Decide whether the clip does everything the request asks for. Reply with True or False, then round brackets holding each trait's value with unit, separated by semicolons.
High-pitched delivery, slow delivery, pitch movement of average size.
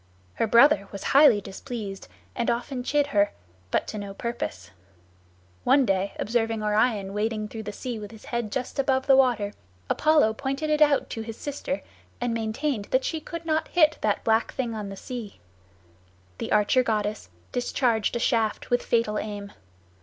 False (230 Hz; 170 wpm; 4.1 semitones)